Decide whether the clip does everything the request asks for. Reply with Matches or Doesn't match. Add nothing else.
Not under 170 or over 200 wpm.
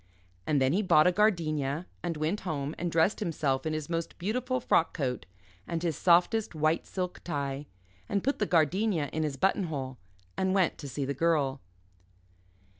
Matches